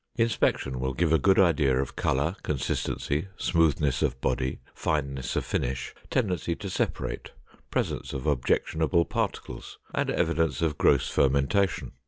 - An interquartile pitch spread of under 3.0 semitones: No, average, 4.0 semitones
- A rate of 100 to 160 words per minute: Yes, slow, 135 wpm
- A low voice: Yes, very low, 75 Hz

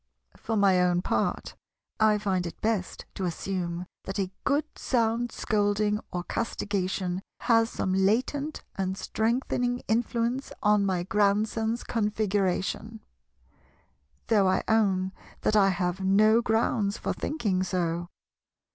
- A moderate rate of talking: No, slow, 120 wpm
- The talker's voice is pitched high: Yes, high, 205 Hz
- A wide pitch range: No, average, 3.1 semitones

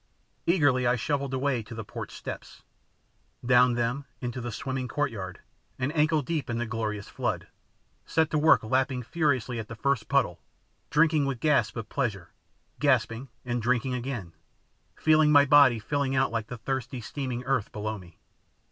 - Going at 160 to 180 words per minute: Yes, average, 165 wpm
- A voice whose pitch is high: No, low, 125 Hz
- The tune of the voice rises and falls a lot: No, average, 3.6 semitones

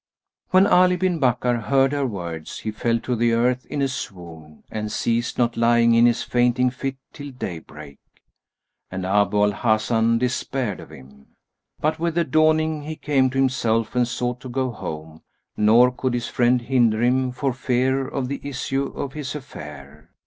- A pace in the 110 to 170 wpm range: No, average, 180 wpm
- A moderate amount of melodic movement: Yes, average, 3.6 semitones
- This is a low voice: Yes, low, 125 Hz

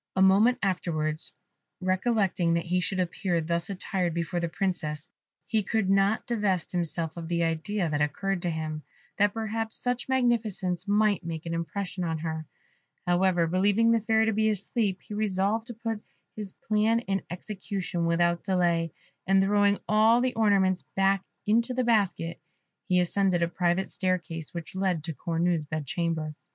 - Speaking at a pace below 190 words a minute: Yes, average, 165 wpm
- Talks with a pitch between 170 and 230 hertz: Yes, medium, 185 Hz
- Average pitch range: Yes, average, 3.8 semitones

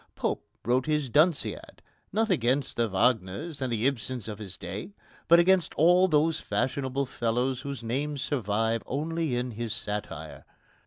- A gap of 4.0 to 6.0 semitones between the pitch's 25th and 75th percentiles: Yes, average, 4.8 semitones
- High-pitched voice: No, low, 130 Hz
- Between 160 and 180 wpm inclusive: No, average, 145 wpm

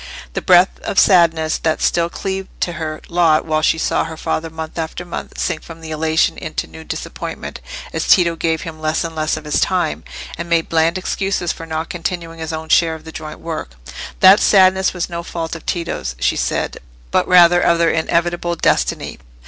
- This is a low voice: No, medium, 165 Hz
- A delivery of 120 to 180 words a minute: No, average, 190 wpm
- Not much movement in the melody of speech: Yes, narrow, 1.6 semitones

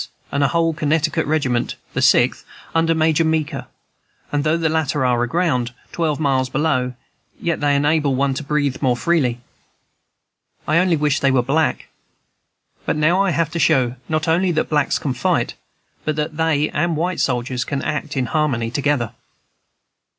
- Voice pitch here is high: No, medium, 150 Hz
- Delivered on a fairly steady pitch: No, average, 3.4 semitones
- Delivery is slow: No, average, 165 wpm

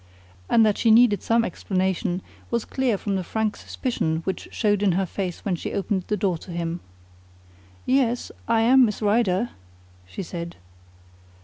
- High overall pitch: Yes, high, 205 Hz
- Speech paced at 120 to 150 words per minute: No, average, 165 wpm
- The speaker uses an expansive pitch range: No, average, 3.9 semitones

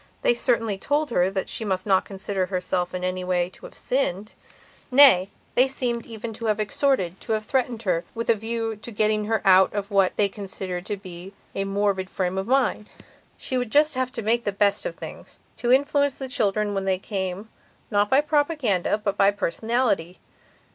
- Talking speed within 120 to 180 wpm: No, average, 195 wpm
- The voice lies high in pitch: Yes, high, 210 Hz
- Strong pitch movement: No, average, 4.0 semitones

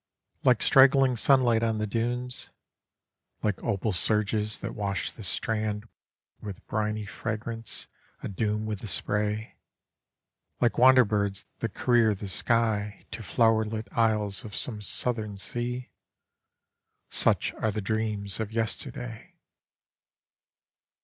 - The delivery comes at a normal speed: No, slow, 115 wpm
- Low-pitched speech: Yes, low, 110 Hz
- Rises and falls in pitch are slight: Yes, narrow, 1.8 semitones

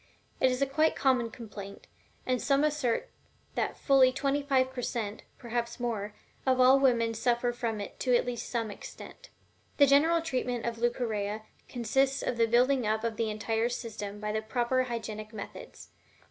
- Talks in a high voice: Yes, high, 240 Hz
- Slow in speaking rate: No, average, 175 wpm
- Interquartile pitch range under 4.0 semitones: Yes, average, 2.8 semitones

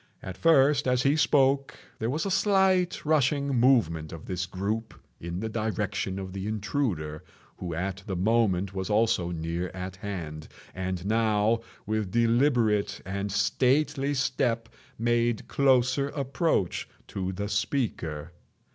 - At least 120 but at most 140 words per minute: Yes, slow, 135 wpm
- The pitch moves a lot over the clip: Yes, wide, 6.0 semitones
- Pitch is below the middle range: Yes, low, 110 Hz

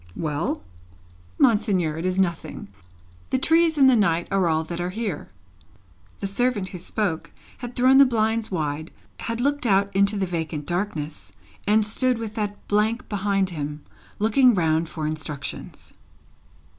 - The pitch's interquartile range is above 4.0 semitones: Yes, wide, 5.5 semitones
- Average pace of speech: Yes, average, 150 wpm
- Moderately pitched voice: No, high, 200 Hz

